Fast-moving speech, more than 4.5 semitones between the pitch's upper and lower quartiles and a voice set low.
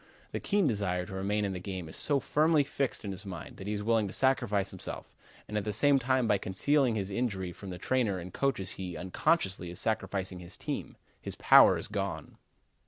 Yes: fast, 215 wpm; wide, 5.5 semitones; low, 105 Hz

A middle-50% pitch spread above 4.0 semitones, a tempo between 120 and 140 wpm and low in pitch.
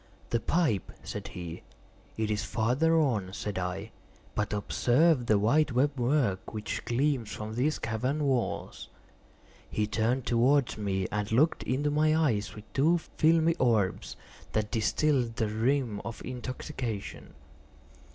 Yes: average, 5.2 semitones; slow, 135 wpm; low, 120 Hz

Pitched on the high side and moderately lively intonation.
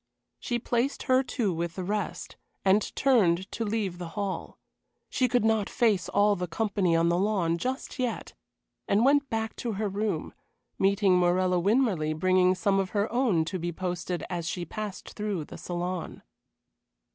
Yes: high, 195 Hz; average, 3.9 semitones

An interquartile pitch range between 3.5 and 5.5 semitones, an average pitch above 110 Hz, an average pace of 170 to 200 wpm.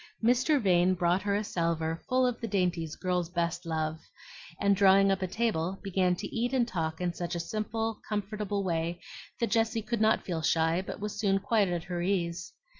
Yes: average, 3.8 semitones; high, 190 Hz; average, 195 wpm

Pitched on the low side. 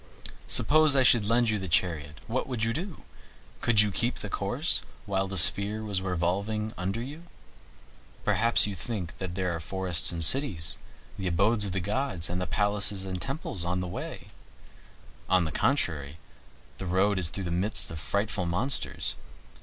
Yes: very low, 95 Hz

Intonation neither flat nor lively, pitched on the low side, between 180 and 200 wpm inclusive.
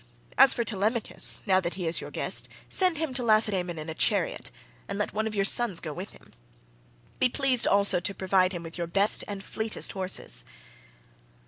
No: average, 4.0 semitones; high, 200 Hz; average, 195 wpm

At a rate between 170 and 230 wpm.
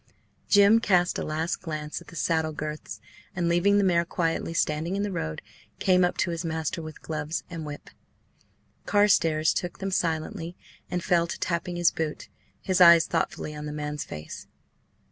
Yes: average, 175 wpm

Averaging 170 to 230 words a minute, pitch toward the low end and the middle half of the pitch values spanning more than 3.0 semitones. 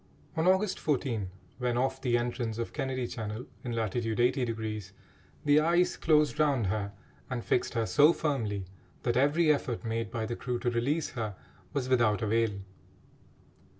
No: average, 155 wpm; low, 120 Hz; average, 3.9 semitones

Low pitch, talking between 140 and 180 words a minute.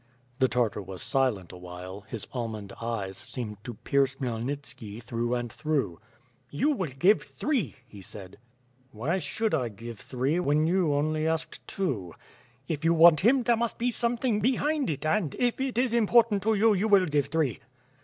No: medium, 145 Hz; average, 175 wpm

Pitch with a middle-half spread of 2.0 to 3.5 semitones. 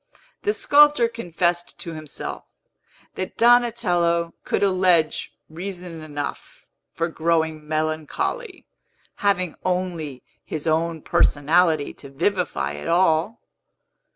Yes: average, 3.2 semitones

